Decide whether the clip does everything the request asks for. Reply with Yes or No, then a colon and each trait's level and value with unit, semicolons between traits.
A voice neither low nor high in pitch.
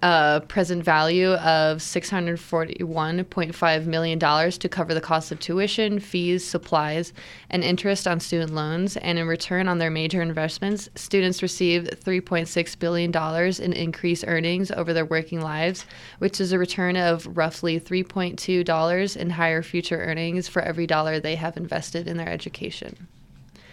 Yes: medium, 170 Hz